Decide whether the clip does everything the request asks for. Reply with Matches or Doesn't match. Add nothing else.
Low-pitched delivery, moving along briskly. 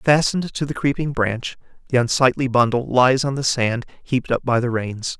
Doesn't match